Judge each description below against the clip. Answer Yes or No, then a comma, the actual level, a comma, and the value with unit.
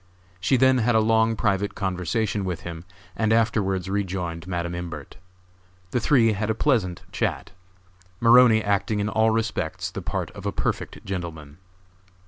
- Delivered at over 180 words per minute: No, average, 155 wpm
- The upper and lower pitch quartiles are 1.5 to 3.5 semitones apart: No, average, 3.9 semitones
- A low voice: Yes, low, 100 Hz